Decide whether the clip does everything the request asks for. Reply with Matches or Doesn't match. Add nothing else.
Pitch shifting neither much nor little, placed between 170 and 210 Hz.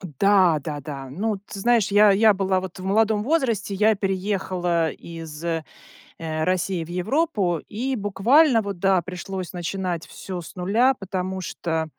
Matches